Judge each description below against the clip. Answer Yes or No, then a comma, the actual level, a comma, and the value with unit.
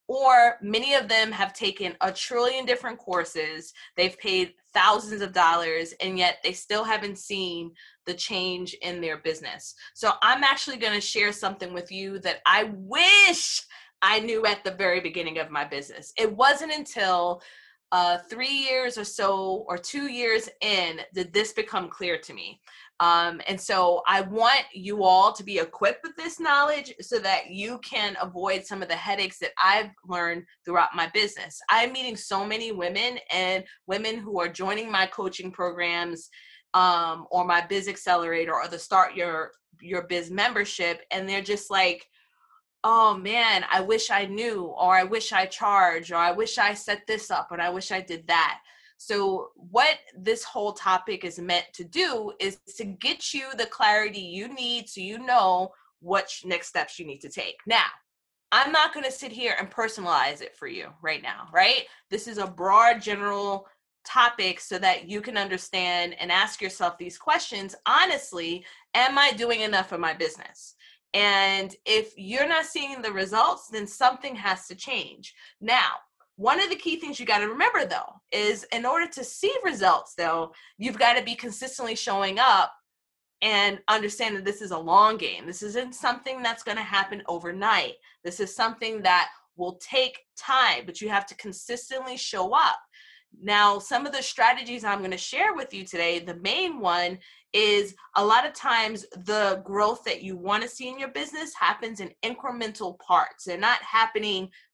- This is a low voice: No, high, 205 Hz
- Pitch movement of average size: Yes, average, 4.7 semitones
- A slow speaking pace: No, average, 180 wpm